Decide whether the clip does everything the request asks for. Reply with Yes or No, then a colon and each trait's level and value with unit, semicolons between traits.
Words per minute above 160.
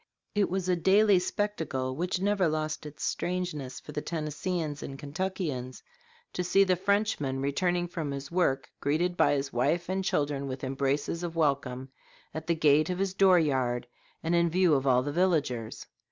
Yes: average, 175 wpm